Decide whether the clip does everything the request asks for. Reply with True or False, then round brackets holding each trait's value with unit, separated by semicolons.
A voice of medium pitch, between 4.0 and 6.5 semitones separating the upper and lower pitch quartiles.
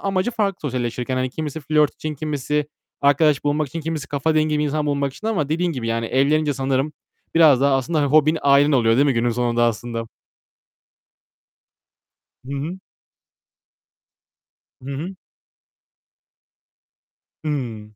False (145 Hz; 3.1 semitones)